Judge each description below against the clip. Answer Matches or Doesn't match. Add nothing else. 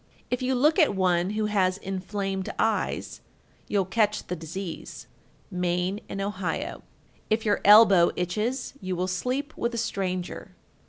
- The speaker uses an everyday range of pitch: Matches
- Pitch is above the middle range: Matches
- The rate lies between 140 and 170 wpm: Matches